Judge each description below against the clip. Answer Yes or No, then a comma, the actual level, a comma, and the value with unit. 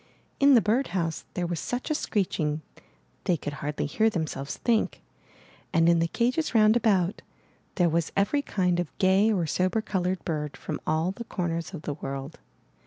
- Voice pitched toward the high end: No, medium, 180 Hz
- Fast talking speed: No, average, 175 wpm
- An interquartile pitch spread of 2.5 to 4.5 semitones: No, average, 5.0 semitones